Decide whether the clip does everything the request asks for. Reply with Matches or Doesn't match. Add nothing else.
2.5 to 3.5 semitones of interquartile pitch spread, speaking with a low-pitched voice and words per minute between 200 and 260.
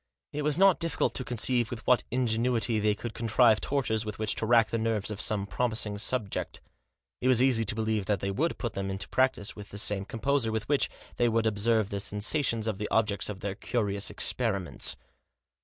Matches